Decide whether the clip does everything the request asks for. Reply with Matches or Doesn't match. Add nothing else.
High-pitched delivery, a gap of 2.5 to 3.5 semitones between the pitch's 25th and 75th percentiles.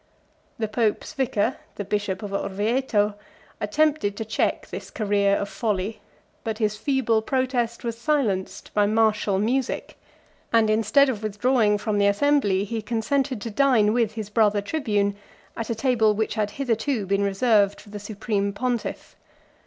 Matches